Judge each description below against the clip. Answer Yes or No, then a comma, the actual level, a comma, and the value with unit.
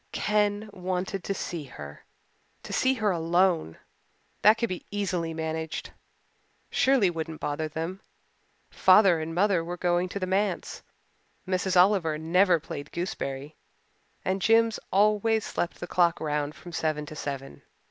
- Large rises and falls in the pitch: No, average, 3.8 semitones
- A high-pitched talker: No, medium, 180 Hz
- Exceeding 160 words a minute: No, average, 140 wpm